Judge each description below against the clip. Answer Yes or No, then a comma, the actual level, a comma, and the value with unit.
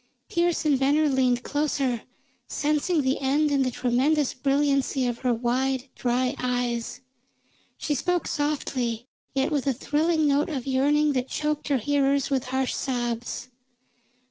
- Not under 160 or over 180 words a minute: No, average, 145 wpm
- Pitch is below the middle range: No, very high, 270 Hz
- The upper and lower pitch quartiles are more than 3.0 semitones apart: No, average, 2.7 semitones